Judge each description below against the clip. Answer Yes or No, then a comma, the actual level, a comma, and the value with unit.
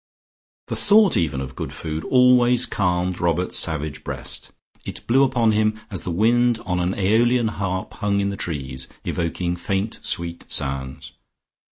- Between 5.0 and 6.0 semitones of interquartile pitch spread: Yes, wide, 5.5 semitones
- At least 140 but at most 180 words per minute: Yes, average, 155 wpm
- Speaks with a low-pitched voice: Yes, very low, 95 Hz